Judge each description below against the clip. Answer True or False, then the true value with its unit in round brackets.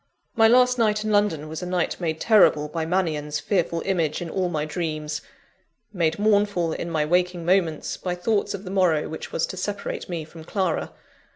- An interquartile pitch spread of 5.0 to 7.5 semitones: False (3.9 semitones)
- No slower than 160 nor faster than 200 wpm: True (190 wpm)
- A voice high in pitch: False (175 Hz)